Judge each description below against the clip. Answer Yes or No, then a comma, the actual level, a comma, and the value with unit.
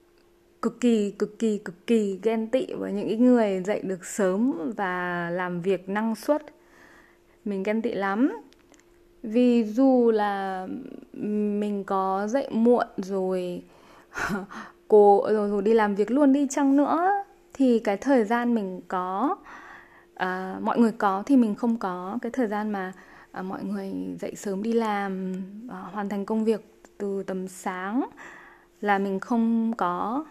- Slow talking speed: Yes, slow, 155 wpm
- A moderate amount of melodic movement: Yes, average, 4.1 semitones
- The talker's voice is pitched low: No, high, 210 Hz